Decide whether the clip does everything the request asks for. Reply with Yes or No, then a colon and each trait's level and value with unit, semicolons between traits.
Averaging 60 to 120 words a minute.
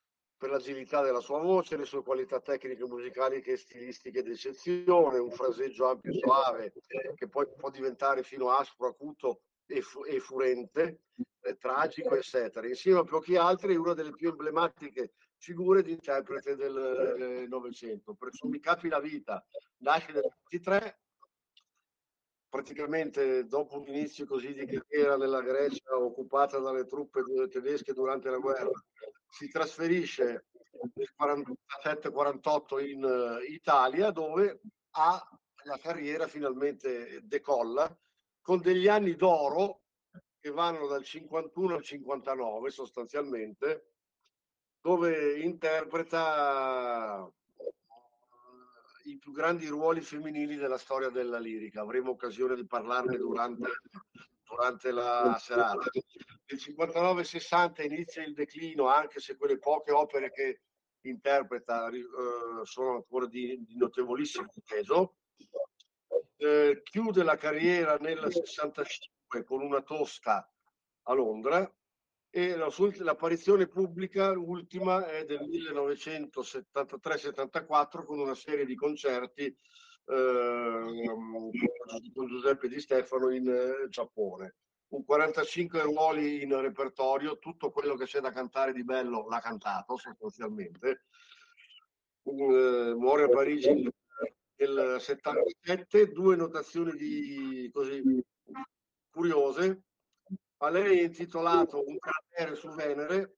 Yes: slow, 115 wpm